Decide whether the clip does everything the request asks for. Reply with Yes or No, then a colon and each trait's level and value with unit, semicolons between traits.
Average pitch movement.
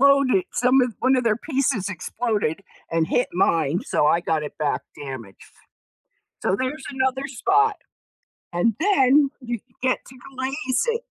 No: wide, 7.5 semitones